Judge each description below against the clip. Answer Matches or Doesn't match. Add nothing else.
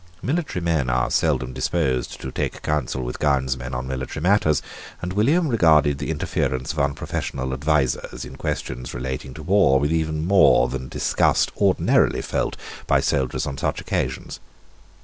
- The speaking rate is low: Doesn't match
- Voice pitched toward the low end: Matches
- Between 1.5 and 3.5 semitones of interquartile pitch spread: Doesn't match